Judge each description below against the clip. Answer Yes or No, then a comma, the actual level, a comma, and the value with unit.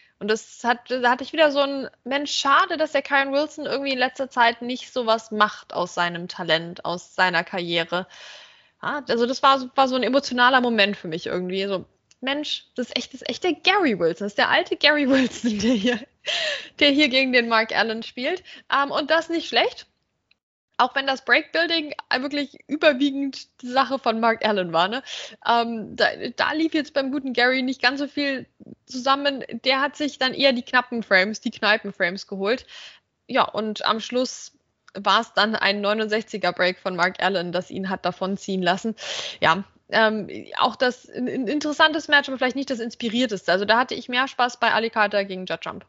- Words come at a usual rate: No, fast, 200 wpm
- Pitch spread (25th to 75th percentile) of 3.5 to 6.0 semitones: Yes, average, 5.2 semitones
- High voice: Yes, high, 245 Hz